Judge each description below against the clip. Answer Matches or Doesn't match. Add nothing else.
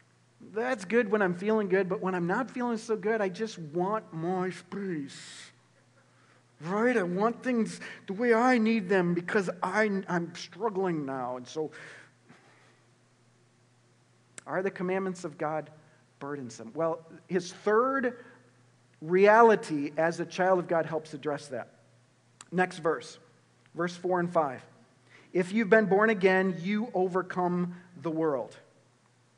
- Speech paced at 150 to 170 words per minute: Doesn't match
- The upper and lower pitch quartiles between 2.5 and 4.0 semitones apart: Doesn't match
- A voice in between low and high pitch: Matches